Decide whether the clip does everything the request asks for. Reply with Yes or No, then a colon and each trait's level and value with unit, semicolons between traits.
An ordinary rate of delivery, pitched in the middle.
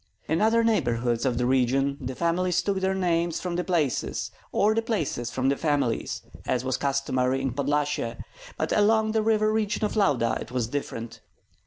Yes: average, 180 wpm; medium, 145 Hz